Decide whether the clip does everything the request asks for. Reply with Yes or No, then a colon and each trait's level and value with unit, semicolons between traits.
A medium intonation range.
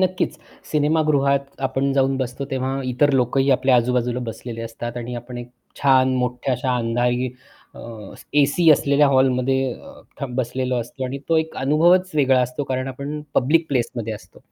No: narrow, 2.1 semitones